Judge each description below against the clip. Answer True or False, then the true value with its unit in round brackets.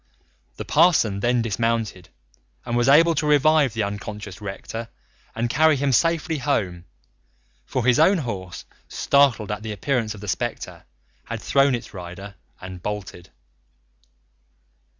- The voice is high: False (115 Hz)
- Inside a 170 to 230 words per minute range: False (135 wpm)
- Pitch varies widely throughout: True (5.7 semitones)